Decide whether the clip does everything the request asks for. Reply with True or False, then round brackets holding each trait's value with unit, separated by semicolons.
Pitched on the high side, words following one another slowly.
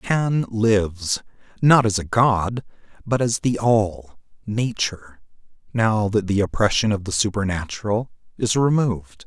False (105 Hz; 130 wpm)